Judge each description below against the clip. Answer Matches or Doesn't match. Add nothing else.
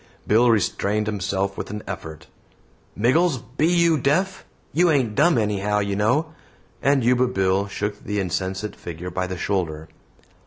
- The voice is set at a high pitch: Doesn't match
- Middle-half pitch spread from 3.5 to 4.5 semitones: Doesn't match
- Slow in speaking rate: Doesn't match